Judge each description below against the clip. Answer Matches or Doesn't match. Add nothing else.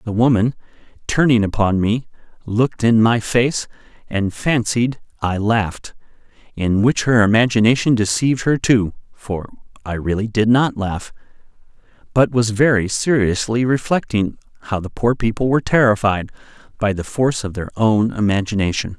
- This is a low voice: Matches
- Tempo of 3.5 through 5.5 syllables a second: Matches